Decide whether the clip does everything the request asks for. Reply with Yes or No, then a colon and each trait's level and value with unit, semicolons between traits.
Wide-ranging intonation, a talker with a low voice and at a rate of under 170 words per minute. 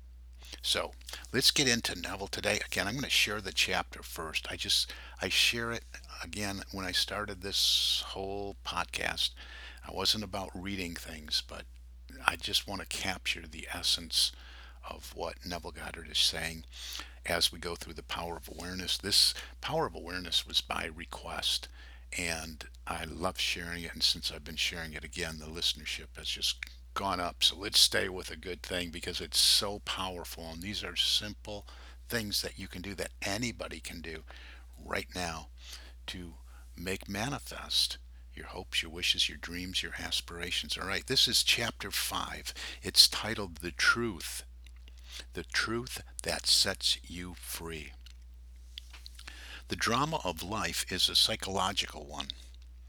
Yes: wide, 6.6 semitones; very low, 80 Hz; average, 160 wpm